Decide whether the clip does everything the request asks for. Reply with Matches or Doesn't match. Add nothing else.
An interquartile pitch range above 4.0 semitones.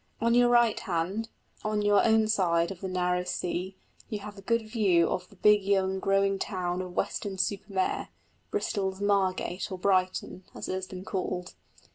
Doesn't match